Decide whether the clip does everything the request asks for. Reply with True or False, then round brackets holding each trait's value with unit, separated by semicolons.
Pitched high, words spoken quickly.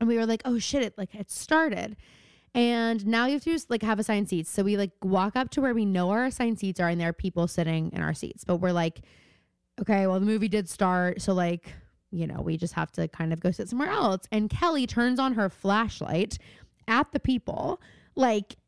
True (205 Hz; 240 wpm)